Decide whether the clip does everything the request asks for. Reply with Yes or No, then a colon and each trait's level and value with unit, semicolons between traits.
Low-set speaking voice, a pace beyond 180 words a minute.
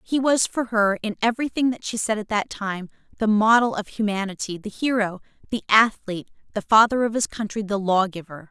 No: high, 210 Hz; average, 200 wpm